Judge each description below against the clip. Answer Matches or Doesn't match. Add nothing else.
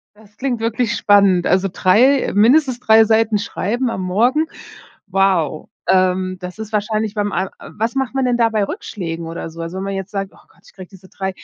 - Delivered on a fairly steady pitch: Doesn't match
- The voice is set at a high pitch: Matches